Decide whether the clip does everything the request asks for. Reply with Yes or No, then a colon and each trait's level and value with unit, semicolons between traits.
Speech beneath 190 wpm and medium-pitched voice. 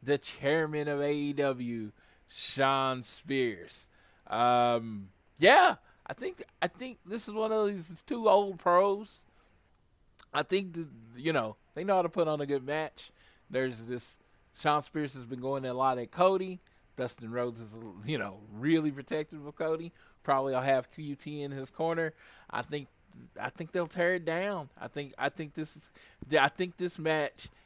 Yes: average, 175 wpm; medium, 150 Hz